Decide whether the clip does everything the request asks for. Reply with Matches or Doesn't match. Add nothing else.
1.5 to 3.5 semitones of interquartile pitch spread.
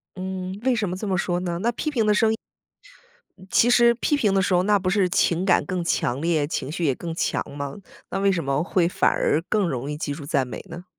Doesn't match